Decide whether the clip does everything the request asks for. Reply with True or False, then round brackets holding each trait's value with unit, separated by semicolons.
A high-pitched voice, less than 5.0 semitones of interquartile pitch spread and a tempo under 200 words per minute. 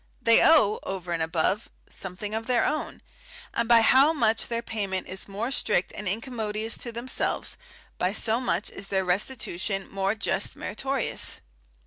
True (215 Hz; 3.5 semitones; 155 wpm)